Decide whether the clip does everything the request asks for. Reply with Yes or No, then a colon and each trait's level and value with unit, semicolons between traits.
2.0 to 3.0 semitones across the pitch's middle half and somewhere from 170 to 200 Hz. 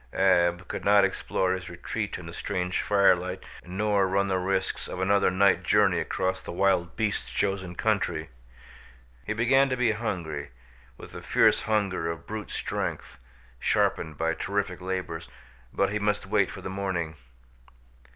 No: narrow, 2.4 semitones; very low, 95 Hz